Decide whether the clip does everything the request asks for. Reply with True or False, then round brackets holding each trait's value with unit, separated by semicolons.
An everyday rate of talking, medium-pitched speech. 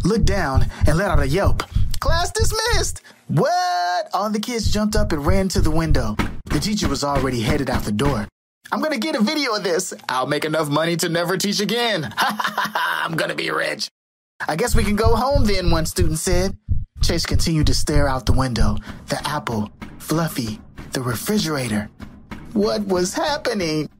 True (180 wpm; 155 Hz)